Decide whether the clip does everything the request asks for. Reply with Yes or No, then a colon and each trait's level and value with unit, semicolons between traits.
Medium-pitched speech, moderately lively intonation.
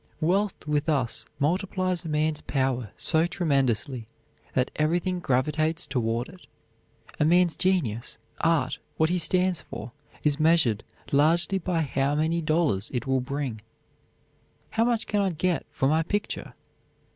Yes: medium, 155 Hz; average, 4.7 semitones